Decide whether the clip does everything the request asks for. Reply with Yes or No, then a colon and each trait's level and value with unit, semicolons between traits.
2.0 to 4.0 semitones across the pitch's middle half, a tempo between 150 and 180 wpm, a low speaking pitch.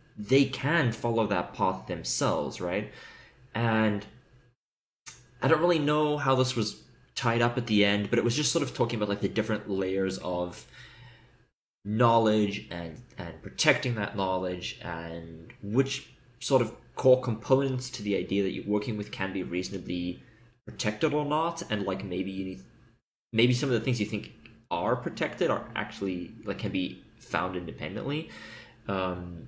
No: average, 4.7 semitones; average, 165 wpm; low, 110 Hz